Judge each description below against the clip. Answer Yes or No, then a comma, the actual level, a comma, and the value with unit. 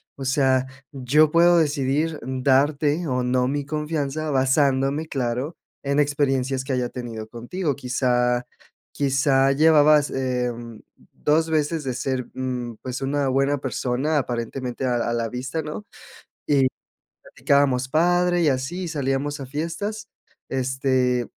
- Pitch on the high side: No, low, 135 Hz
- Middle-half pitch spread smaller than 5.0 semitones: Yes, average, 2.8 semitones